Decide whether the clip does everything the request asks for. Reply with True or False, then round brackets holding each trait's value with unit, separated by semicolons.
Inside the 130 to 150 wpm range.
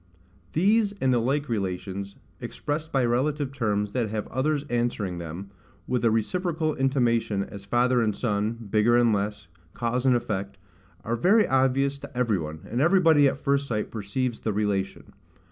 False (160 wpm)